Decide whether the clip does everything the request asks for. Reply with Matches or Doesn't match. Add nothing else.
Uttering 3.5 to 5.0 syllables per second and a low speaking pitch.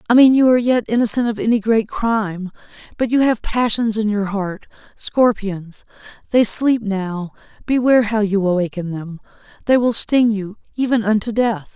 Doesn't match